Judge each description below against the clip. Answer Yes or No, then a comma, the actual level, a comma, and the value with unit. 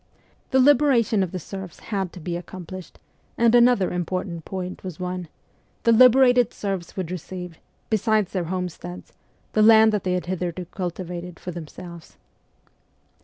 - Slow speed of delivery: No, average, 145 wpm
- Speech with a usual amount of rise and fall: Yes, average, 3.6 semitones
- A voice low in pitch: No, medium, 185 Hz